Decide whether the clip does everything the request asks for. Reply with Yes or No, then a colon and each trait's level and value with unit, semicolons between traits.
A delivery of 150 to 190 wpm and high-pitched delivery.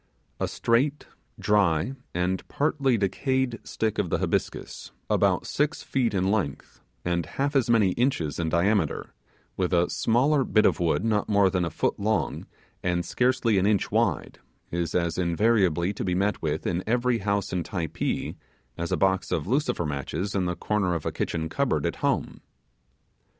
No: average, 170 wpm; low, 100 Hz